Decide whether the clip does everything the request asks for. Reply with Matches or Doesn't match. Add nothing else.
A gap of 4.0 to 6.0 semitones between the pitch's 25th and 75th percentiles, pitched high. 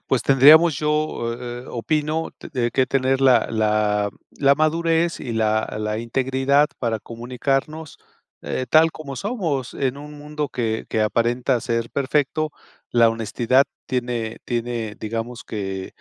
Doesn't match